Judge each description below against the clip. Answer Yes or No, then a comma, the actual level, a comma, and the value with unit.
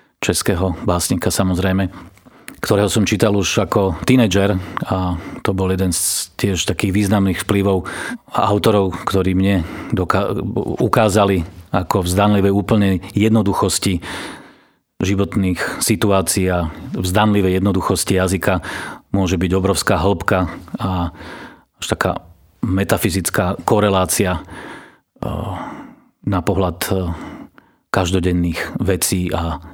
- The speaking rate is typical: No, slow, 95 wpm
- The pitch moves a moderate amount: No, narrow, 1.8 semitones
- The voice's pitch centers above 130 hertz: No, very low, 95 Hz